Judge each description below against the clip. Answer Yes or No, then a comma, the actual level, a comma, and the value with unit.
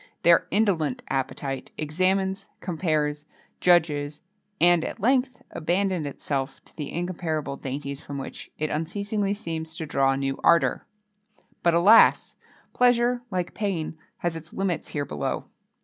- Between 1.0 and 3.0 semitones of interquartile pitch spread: No, average, 4.5 semitones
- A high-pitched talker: No, medium, 165 Hz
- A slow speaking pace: Yes, slow, 130 wpm